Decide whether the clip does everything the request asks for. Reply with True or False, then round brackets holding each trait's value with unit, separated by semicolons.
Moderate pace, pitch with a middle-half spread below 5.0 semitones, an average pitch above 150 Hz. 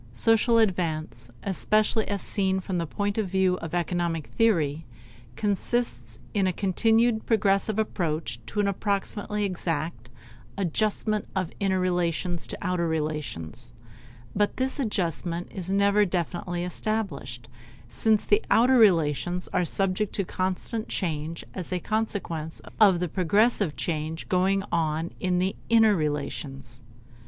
False (130 wpm; 4.1 semitones; 185 Hz)